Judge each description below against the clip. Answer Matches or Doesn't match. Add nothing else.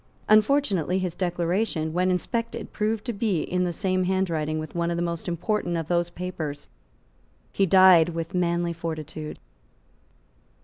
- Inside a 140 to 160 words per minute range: Matches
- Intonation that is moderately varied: Doesn't match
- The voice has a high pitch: Doesn't match